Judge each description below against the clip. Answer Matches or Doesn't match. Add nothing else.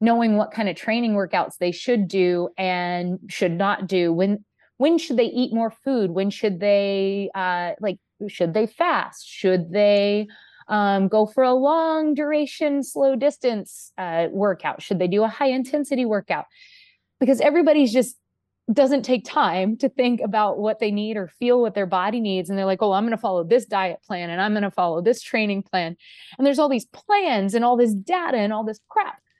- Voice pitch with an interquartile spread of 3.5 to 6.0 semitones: Matches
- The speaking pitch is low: Doesn't match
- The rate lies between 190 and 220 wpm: Matches